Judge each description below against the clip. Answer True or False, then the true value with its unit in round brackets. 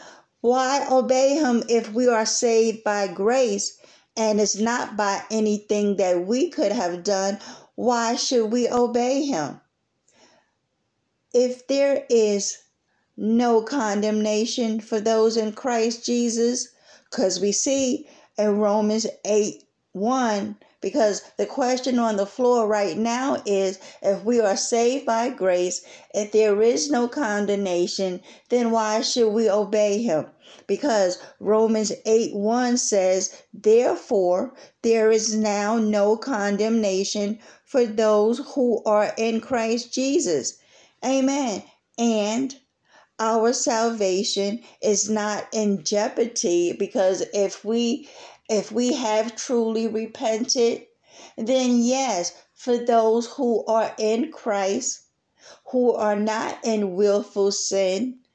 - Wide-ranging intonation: False (2.9 semitones)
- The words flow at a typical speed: False (120 wpm)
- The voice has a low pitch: False (225 Hz)